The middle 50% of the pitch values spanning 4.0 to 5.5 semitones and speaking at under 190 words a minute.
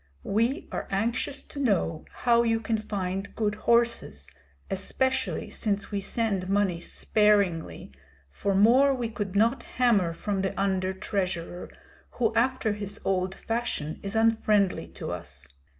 No: average, 3.4 semitones; slow, 135 wpm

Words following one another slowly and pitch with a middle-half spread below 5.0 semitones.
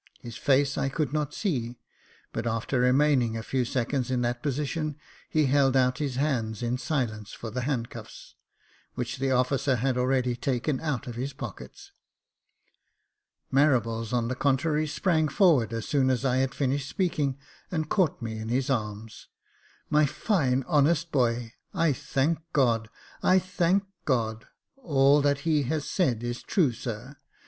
No: average, 160 wpm; average, 3.6 semitones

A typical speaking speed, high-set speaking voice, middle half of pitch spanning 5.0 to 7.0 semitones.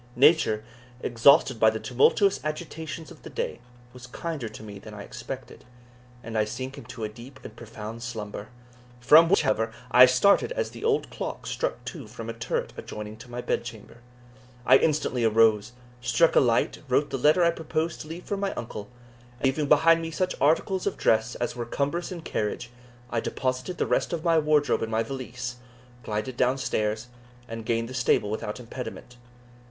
No: average, 185 wpm; low, 125 Hz; wide, 5.5 semitones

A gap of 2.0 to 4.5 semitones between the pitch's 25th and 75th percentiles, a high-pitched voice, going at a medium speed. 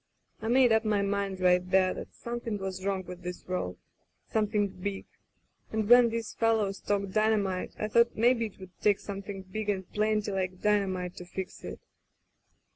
Yes: narrow, 2.6 semitones; high, 200 Hz; average, 185 wpm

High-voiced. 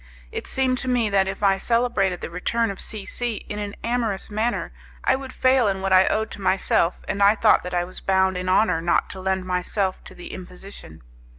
Yes: high, 195 Hz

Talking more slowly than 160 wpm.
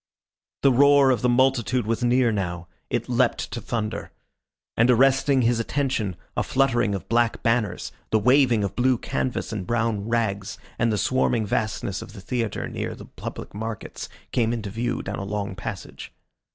No: average, 170 wpm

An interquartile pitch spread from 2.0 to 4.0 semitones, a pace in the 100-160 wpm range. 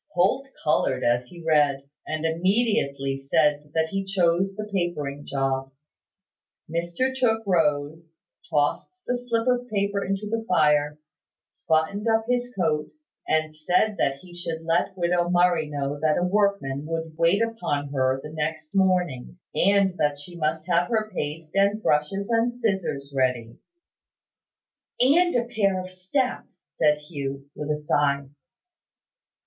No: average, 5.1 semitones; average, 145 wpm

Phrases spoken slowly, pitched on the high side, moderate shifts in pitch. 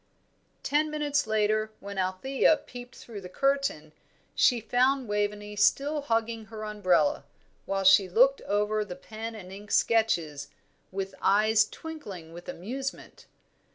Yes: slow, 130 wpm; high, 215 Hz; average, 4.7 semitones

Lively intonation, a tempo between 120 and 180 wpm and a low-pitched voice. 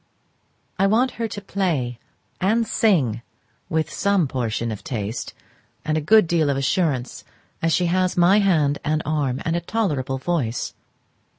No: wide, 6.3 semitones; average, 155 wpm; medium, 160 Hz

